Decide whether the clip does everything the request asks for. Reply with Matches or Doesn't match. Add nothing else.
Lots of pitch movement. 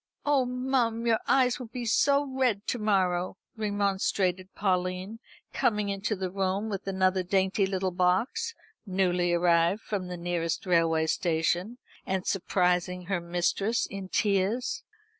Doesn't match